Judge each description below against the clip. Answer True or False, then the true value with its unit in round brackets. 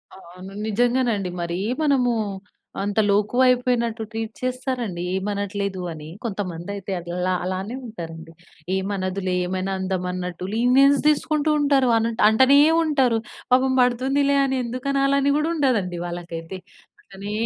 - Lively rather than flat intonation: True (5.7 semitones)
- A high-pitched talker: True (220 Hz)